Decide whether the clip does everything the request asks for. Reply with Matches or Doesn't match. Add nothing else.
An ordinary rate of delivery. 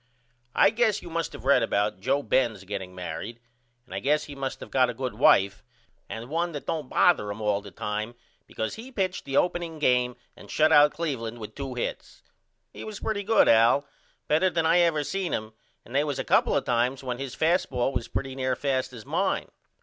Doesn't match